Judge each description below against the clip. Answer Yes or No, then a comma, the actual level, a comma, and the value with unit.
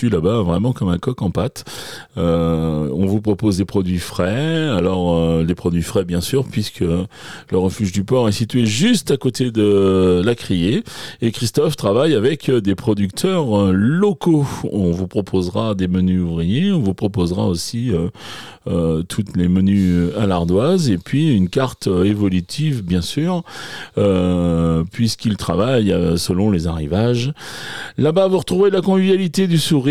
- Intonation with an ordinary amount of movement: No, wide, 6.6 semitones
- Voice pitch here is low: Yes, low, 100 Hz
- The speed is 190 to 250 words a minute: No, average, 155 wpm